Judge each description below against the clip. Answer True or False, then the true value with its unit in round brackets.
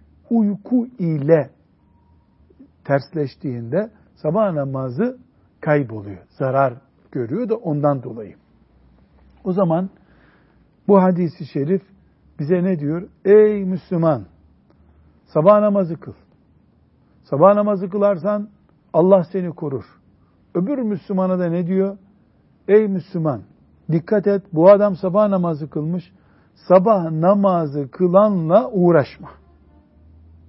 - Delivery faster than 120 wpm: False (95 wpm)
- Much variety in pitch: True (7.3 semitones)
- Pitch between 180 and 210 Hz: False (170 Hz)